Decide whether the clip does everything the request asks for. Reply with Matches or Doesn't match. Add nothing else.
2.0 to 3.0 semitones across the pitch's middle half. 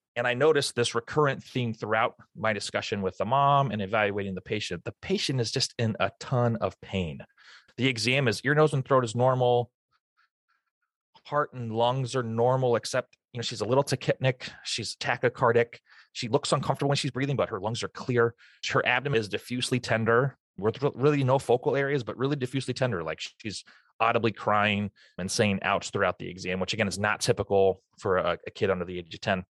Doesn't match